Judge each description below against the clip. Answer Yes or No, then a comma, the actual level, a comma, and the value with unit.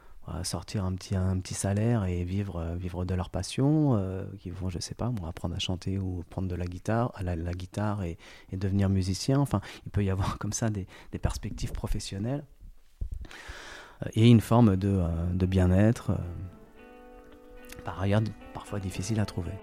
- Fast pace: No, average, 175 wpm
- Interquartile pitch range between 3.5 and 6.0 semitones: No, average, 2.9 semitones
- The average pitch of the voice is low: Yes, very low, 95 Hz